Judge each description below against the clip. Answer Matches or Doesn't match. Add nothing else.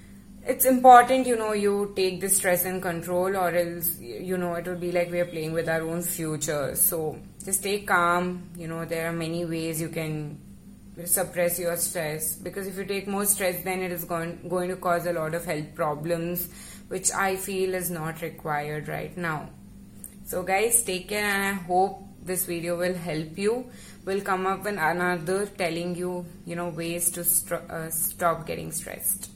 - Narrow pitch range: Matches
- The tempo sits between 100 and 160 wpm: Doesn't match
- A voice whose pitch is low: Doesn't match